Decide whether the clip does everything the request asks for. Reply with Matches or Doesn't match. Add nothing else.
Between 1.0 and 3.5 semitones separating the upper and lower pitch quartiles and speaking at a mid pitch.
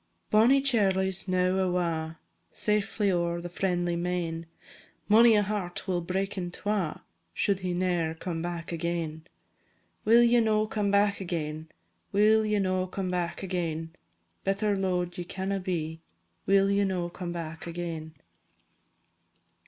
Matches